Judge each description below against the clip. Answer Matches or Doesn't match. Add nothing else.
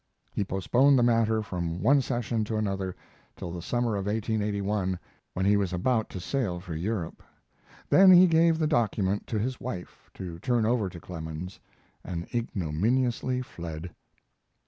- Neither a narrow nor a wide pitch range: Matches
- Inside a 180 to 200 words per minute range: Doesn't match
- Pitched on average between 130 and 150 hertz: Doesn't match